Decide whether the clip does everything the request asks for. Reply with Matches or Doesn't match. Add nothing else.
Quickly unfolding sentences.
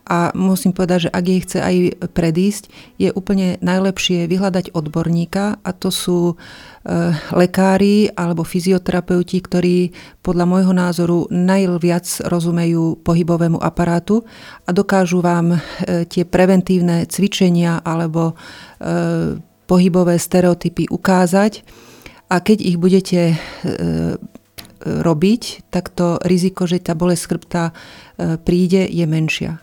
Doesn't match